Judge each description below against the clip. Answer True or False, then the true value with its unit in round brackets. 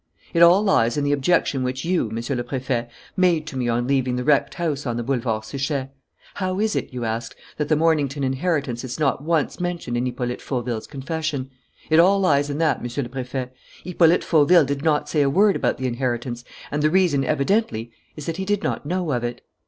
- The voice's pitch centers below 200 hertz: True (140 Hz)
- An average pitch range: True (4.8 semitones)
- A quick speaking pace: True (215 wpm)